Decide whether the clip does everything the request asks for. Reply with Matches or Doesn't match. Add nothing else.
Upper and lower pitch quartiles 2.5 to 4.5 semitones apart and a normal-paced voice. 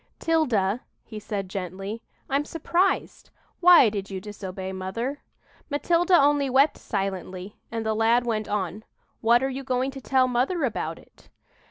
Doesn't match